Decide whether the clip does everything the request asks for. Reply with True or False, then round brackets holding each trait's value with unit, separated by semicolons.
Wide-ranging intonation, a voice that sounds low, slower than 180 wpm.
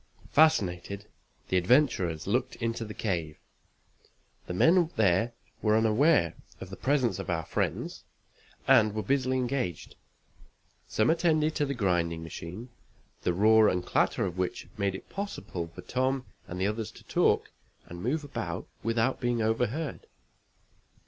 True (6.1 semitones; 110 Hz; 140 wpm)